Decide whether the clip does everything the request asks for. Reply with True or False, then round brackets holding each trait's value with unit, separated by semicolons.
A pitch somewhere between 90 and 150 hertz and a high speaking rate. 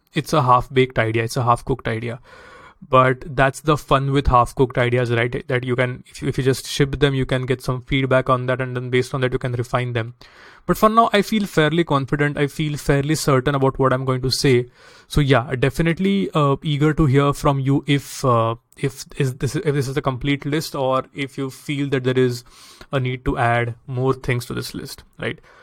True (135 Hz; 225 wpm)